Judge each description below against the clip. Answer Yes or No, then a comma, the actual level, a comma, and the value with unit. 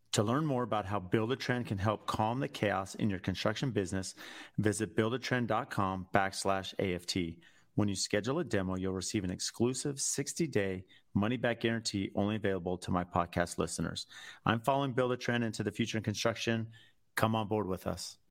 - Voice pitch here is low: Yes, low, 105 Hz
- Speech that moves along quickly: No, average, 175 wpm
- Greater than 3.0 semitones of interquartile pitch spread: Yes, average, 3.4 semitones